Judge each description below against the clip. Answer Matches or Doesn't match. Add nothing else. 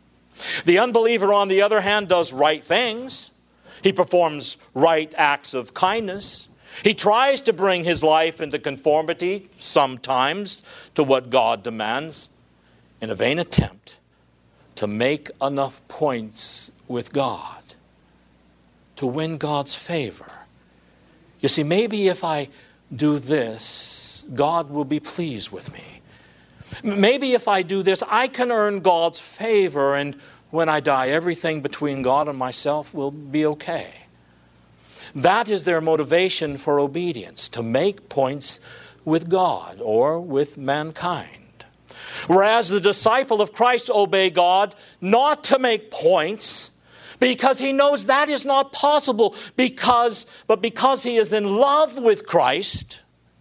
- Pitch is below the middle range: Doesn't match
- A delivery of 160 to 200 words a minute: Doesn't match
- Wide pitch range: Matches